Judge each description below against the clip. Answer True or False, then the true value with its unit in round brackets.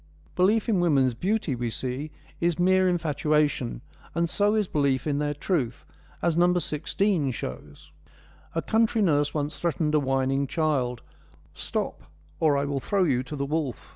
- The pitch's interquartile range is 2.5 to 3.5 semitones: False (4.5 semitones)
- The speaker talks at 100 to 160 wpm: False (170 wpm)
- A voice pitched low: False (150 Hz)